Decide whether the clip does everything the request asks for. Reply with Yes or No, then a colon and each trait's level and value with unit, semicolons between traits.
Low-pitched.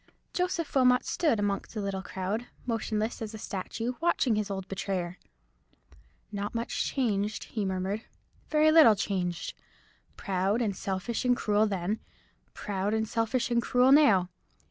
No: high, 215 Hz